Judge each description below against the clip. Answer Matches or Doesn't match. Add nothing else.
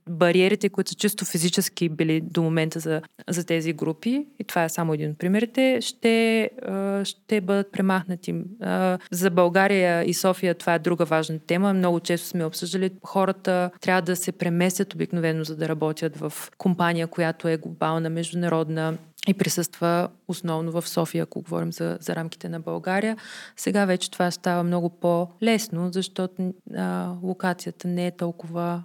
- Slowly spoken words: Doesn't match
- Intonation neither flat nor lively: Doesn't match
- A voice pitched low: Doesn't match